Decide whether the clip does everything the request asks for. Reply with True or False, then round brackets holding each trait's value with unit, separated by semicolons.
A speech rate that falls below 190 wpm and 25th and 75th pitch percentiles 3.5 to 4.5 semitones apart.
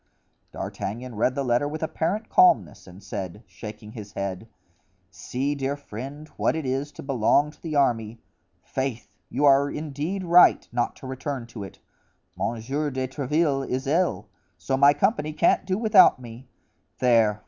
True (160 wpm; 4.2 semitones)